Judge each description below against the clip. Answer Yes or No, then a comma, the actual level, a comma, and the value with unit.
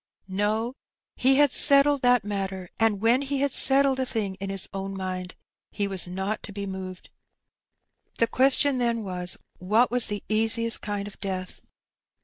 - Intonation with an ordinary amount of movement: Yes, average, 4.4 semitones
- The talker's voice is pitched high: Yes, high, 210 Hz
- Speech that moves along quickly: No, average, 165 wpm